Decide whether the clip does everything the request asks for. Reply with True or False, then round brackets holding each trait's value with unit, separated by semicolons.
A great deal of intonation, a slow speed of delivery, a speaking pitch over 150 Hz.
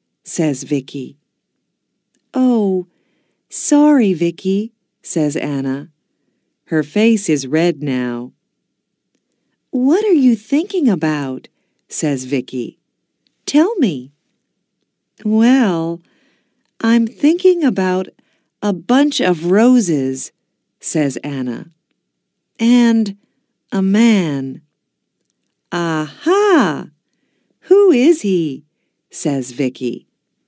True (9.0 semitones; 80 wpm; 185 Hz)